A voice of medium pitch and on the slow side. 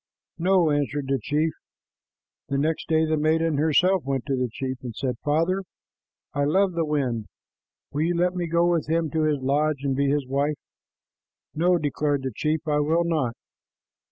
No: medium, 150 Hz; average, 180 wpm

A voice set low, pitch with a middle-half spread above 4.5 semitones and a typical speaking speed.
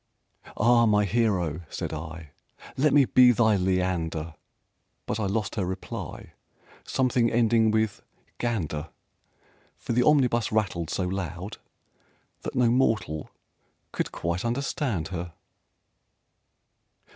No: low, 105 Hz; average, 5.1 semitones; slow, 110 wpm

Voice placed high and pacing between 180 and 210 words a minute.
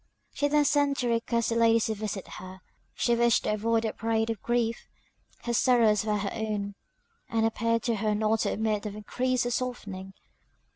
Yes: high, 225 Hz; average, 190 wpm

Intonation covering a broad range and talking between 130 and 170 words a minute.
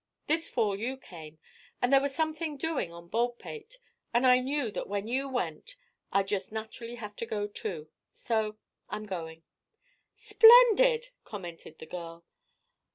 Yes: wide, 6.5 semitones; average, 150 wpm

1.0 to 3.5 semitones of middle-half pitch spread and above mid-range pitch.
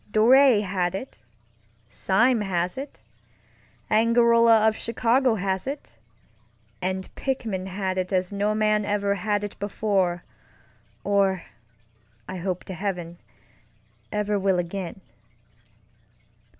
Yes: average, 3.0 semitones; high, 200 Hz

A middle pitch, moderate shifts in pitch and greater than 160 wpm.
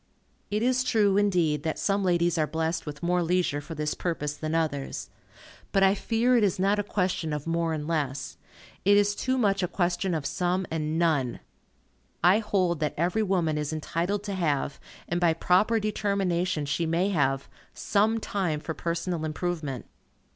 Yes: medium, 175 Hz; average, 4.1 semitones; average, 175 wpm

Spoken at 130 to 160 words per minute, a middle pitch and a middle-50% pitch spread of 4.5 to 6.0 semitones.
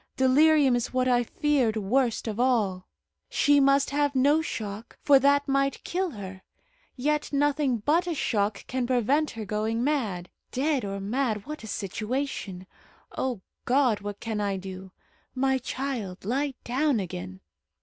No: average, 150 wpm; very high, 255 Hz; average, 5.1 semitones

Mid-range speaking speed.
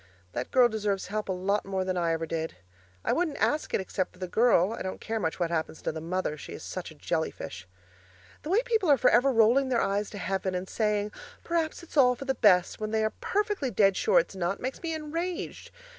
No: fast, 240 wpm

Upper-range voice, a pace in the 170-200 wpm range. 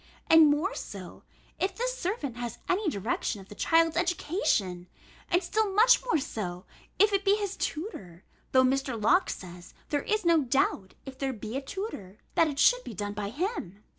Yes: very high, 290 Hz; average, 185 wpm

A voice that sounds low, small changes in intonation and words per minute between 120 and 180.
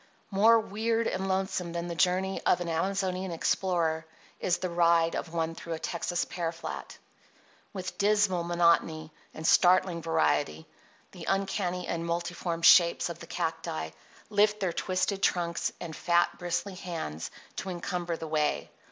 No: medium, 175 Hz; narrow, 2.2 semitones; average, 150 wpm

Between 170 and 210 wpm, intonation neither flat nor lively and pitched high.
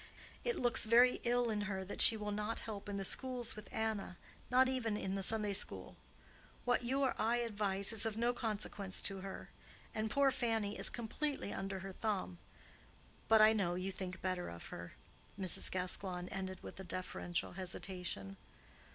Yes: average, 175 wpm; average, 3.4 semitones; high, 205 Hz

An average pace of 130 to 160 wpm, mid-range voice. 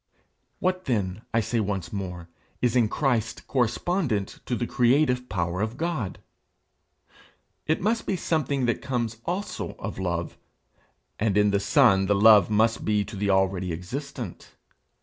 No: average, 150 wpm; low, 110 Hz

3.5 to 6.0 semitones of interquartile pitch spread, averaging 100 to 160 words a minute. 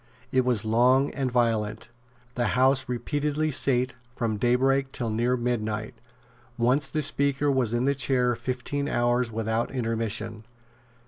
No: average, 2.8 semitones; slow, 135 wpm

